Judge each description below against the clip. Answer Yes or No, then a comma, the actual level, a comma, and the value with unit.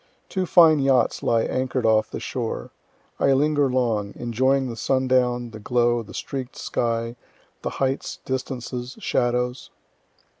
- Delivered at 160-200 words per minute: No, slow, 135 wpm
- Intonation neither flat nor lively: No, narrow, 2.1 semitones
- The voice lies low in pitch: Yes, low, 125 Hz